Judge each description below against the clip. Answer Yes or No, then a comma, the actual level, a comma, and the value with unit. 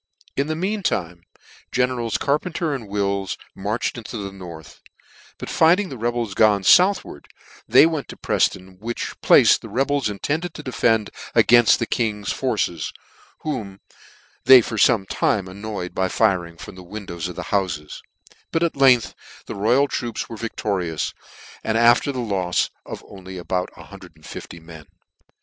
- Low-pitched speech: Yes, low, 110 Hz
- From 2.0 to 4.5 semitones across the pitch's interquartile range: No, wide, 5.6 semitones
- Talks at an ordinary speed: Yes, average, 150 wpm